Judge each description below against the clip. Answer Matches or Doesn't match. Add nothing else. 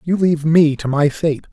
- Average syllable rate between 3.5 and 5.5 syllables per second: Matches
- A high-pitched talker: Doesn't match